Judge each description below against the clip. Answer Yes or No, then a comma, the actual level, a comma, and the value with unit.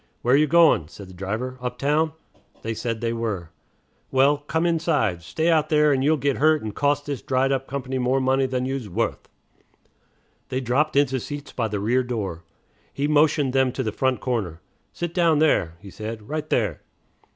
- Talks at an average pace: Yes, average, 185 wpm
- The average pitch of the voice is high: No, low, 130 Hz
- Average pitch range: Yes, average, 4.5 semitones